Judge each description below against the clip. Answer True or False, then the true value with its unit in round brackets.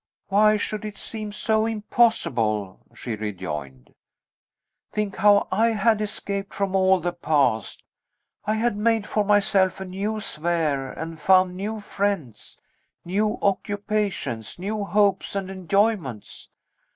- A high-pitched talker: True (195 Hz)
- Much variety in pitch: False (4.5 semitones)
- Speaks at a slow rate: True (125 wpm)